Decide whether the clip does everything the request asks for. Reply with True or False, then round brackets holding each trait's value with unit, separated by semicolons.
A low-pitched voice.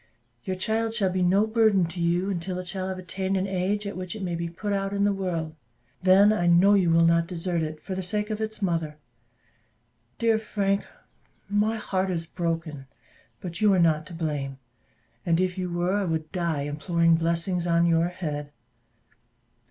False (180 Hz)